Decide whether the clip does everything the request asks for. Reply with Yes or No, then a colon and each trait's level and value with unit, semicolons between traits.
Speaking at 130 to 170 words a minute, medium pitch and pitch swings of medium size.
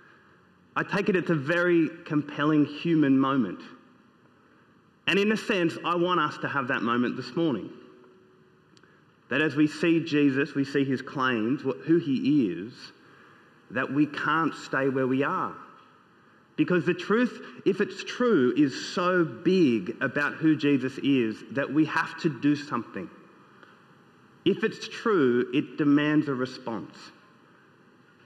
Yes: average, 140 wpm; medium, 160 Hz; average, 4.2 semitones